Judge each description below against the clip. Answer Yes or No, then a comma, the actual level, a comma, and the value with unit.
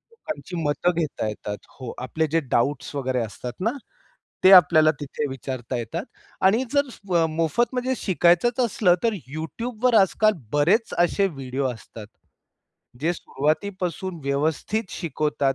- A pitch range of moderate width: No, wide, 6.3 semitones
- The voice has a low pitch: No, medium, 160 Hz